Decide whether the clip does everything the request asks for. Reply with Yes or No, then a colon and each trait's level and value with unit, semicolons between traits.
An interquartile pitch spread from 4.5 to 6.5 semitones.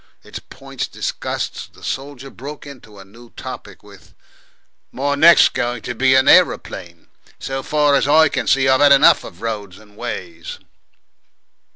Yes: average, 4.8 semitones